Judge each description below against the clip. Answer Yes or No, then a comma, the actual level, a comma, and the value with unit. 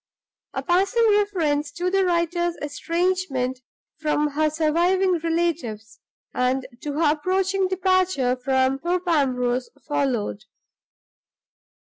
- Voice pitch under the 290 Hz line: No, very high, 320 Hz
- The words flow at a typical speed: No, slow, 100 wpm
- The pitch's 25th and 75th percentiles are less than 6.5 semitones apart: Yes, average, 5.3 semitones